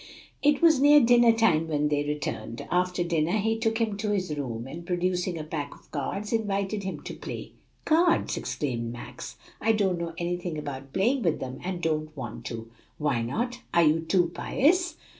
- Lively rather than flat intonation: Yes, wide, 6.7 semitones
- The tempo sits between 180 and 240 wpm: Yes, average, 185 wpm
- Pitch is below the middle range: No, medium, 175 Hz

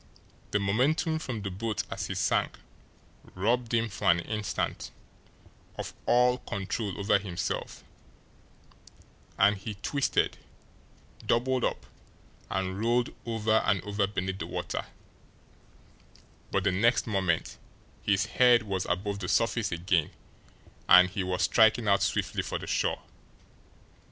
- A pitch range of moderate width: Yes, average, 3.4 semitones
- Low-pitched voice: Yes, low, 105 Hz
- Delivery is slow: Yes, slow, 125 wpm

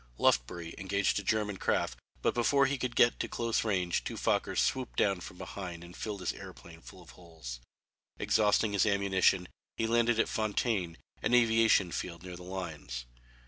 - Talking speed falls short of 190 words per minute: Yes, average, 175 wpm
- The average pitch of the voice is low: Yes, very low, 95 Hz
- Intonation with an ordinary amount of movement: Yes, average, 4.3 semitones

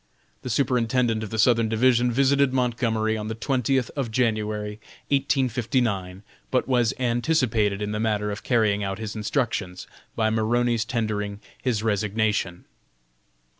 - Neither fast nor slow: No, slow, 130 wpm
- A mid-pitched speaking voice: No, low, 110 Hz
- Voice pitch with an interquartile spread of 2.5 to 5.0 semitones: Yes, average, 2.9 semitones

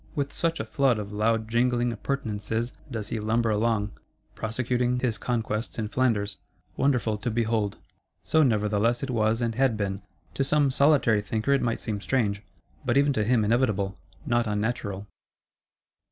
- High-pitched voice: No, low, 115 Hz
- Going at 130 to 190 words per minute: Yes, average, 155 wpm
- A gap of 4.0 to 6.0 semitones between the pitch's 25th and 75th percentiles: No, average, 2.9 semitones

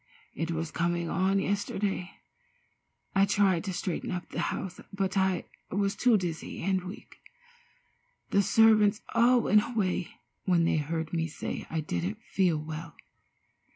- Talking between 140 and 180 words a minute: Yes, average, 145 wpm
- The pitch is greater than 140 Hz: Yes, medium, 185 Hz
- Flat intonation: No, average, 3.3 semitones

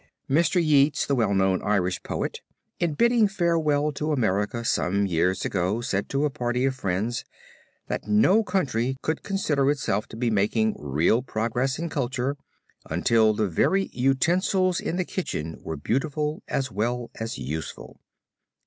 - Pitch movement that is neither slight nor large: No, wide, 6.6 semitones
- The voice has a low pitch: Yes, low, 125 Hz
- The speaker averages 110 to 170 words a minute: Yes, average, 150 wpm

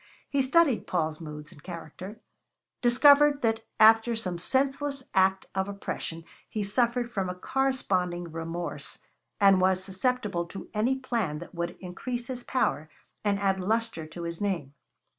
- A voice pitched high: Yes, high, 195 Hz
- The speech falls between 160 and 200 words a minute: No, average, 145 wpm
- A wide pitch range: Yes, wide, 5.7 semitones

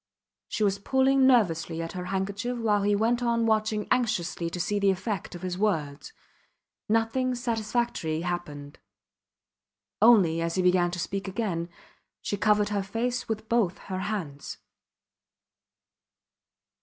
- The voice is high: Yes, high, 200 Hz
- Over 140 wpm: No, slow, 135 wpm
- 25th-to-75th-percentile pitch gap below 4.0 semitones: No, average, 4.4 semitones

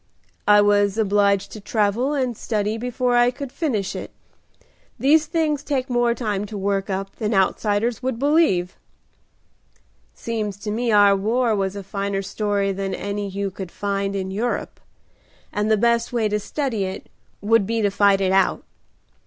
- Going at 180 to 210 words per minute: No, average, 165 wpm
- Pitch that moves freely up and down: No, average, 3.3 semitones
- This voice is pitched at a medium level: No, high, 210 Hz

